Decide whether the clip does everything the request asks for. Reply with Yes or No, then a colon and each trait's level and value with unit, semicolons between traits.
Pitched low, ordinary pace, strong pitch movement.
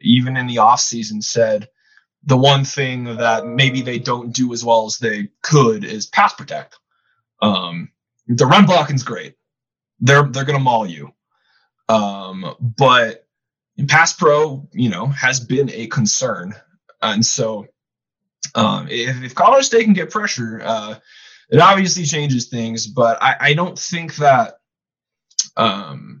No: low, 130 Hz; average, 145 wpm; average, 4.6 semitones